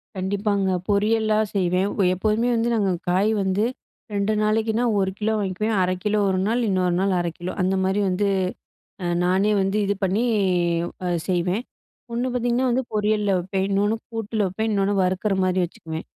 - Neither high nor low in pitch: No, high, 200 Hz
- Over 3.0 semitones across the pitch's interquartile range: No, narrow, 2.5 semitones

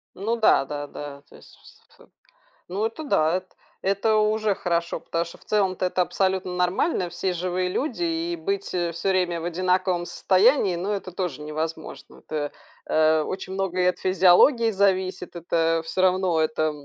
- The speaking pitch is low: No, medium, 185 Hz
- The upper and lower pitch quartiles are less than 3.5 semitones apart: Yes, average, 2.8 semitones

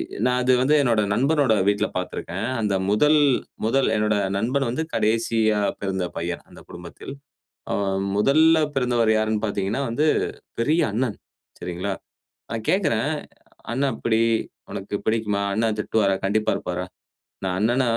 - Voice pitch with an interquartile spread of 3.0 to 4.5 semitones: Yes, average, 4.2 semitones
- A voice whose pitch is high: No, low, 110 Hz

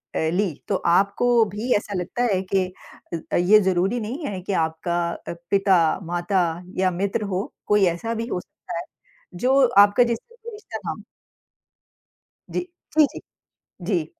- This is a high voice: Yes, high, 195 Hz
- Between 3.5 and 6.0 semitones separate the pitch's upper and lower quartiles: Yes, average, 3.9 semitones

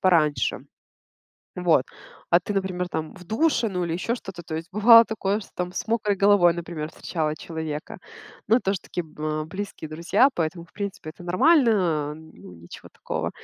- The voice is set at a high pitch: No, medium, 180 Hz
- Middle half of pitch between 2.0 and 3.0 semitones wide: No, average, 4.3 semitones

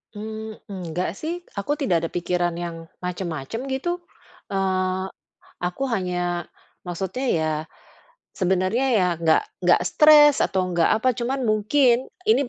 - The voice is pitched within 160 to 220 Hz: Yes, high, 190 Hz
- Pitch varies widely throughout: Yes, wide, 6.4 semitones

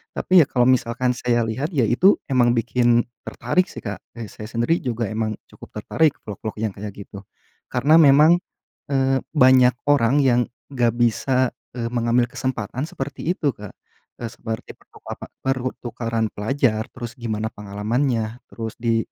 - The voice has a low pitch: Yes, low, 120 Hz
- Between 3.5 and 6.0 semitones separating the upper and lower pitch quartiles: No, average, 2.8 semitones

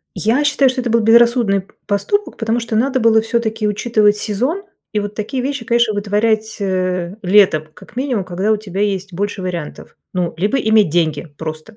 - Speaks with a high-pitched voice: Yes, high, 215 Hz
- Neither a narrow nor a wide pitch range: Yes, average, 3.3 semitones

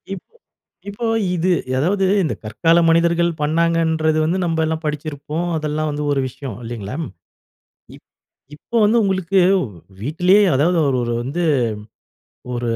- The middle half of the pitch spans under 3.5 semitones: Yes, average, 3.1 semitones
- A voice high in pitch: No, medium, 160 Hz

